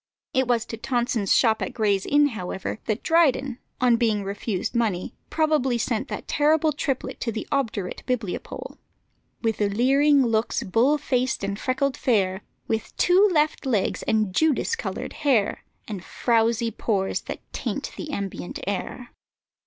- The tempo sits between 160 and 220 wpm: No, average, 145 wpm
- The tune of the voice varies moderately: Yes, average, 4.7 semitones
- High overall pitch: Yes, high, 235 Hz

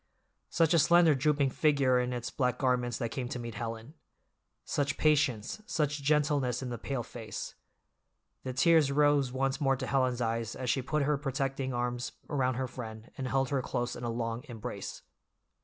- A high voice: No, low, 130 Hz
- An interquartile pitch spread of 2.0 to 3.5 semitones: Yes, average, 2.7 semitones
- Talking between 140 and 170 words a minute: No, average, 180 wpm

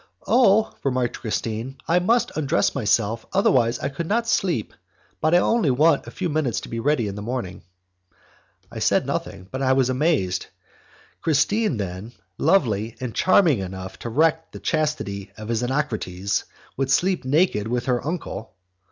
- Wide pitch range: Yes, wide, 6.6 semitones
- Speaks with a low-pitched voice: Yes, low, 130 Hz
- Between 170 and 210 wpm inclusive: No, average, 160 wpm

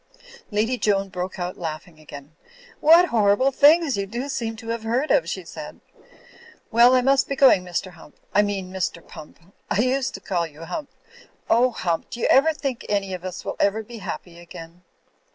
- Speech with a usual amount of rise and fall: No, wide, 5.7 semitones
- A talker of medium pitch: No, high, 205 Hz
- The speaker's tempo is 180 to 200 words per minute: Yes, average, 190 wpm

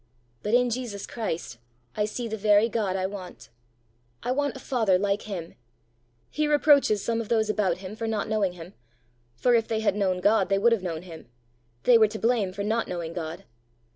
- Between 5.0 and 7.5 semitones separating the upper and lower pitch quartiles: No, average, 3.7 semitones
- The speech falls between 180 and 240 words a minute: Yes, average, 200 wpm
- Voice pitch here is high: Yes, high, 210 Hz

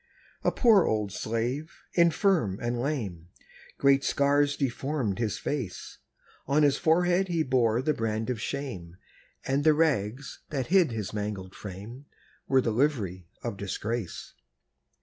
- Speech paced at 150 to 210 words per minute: No, slow, 135 wpm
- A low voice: Yes, low, 125 Hz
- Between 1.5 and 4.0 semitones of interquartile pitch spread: No, wide, 5.6 semitones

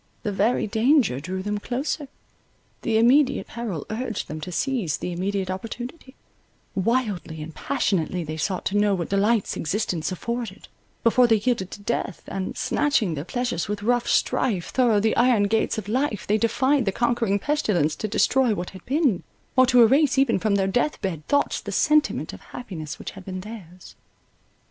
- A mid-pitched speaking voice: No, high, 215 Hz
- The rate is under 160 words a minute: No, average, 175 wpm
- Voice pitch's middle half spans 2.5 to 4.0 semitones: No, average, 4.8 semitones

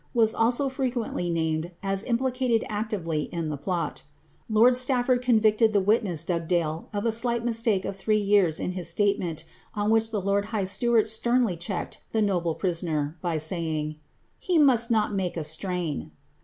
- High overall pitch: Yes, high, 200 Hz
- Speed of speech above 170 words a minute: No, average, 150 wpm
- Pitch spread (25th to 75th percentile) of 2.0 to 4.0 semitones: No, average, 5.2 semitones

